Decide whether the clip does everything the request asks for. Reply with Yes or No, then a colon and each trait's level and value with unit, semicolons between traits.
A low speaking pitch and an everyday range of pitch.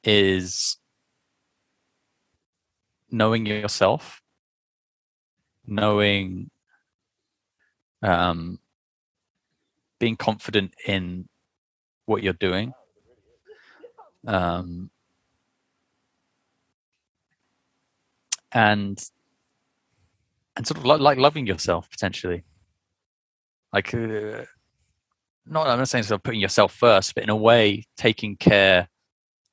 Yes: low, 105 Hz; average, 3.9 semitones